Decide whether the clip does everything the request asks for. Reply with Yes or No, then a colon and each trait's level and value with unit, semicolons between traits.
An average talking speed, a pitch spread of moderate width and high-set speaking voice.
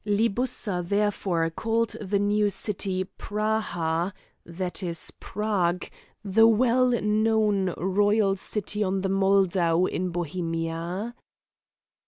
No: slow, 100 wpm; average, 3.0 semitones; high, 195 Hz